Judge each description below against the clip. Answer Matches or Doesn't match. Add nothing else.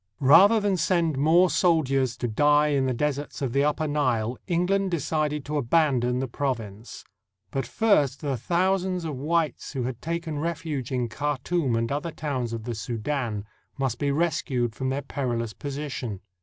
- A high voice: Doesn't match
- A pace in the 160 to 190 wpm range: Matches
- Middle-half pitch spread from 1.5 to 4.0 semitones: Doesn't match